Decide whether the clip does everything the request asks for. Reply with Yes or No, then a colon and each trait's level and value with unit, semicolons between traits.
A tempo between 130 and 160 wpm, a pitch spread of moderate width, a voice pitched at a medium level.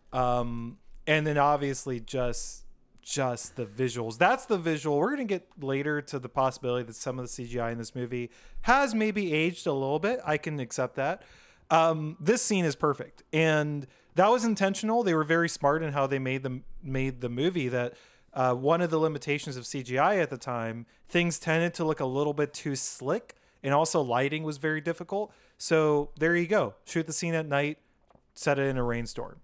No: average, 200 wpm; average, 4.2 semitones; medium, 145 Hz